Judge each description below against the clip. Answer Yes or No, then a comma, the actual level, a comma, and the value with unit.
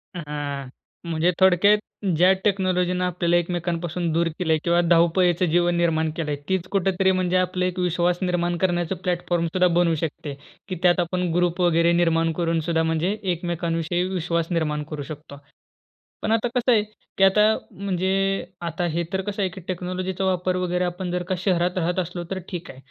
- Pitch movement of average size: No, narrow, 1.6 semitones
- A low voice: No, medium, 175 Hz